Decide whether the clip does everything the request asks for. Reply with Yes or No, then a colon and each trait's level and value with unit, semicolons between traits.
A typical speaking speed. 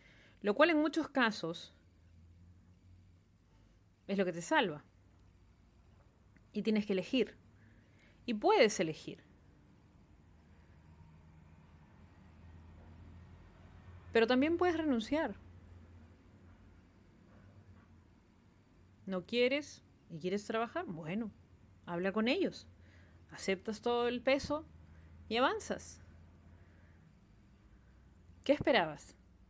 No: slow, 75 wpm